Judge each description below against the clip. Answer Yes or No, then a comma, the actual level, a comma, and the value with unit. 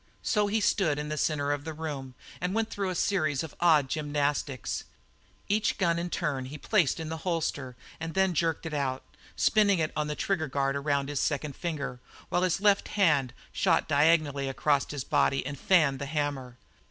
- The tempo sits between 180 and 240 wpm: Yes, average, 190 wpm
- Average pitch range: Yes, average, 3.6 semitones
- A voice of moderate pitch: Yes, medium, 150 Hz